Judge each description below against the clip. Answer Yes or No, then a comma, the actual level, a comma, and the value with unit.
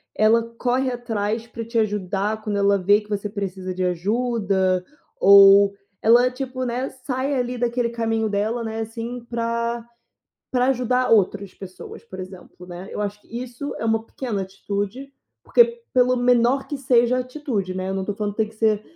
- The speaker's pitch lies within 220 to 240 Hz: Yes, high, 225 Hz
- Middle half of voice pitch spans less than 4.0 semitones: Yes, average, 3.6 semitones